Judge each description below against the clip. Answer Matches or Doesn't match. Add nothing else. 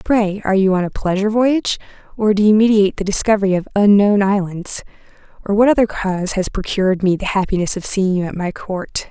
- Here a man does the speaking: Doesn't match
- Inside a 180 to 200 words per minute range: Matches